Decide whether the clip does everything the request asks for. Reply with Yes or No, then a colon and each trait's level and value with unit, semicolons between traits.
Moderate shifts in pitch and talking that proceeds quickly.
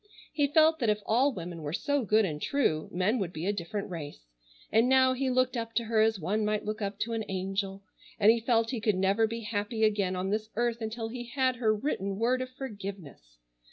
Yes: average, 3.8 semitones; fast, 225 wpm